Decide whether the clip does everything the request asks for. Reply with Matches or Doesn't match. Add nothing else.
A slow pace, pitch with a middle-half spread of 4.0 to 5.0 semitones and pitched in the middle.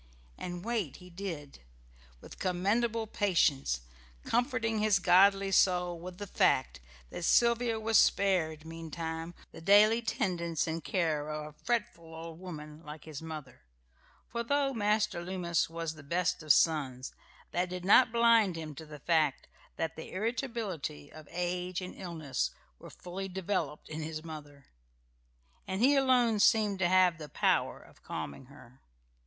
Doesn't match